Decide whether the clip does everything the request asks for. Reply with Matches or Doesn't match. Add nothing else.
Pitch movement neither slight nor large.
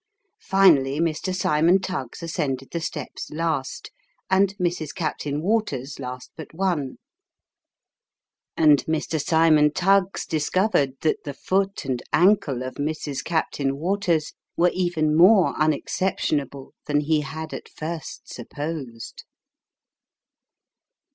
Matches